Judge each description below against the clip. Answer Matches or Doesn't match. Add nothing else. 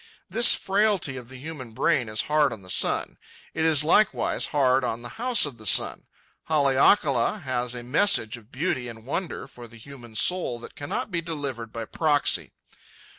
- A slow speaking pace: Doesn't match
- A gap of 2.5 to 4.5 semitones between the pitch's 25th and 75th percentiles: Doesn't match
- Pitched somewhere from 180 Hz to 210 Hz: Doesn't match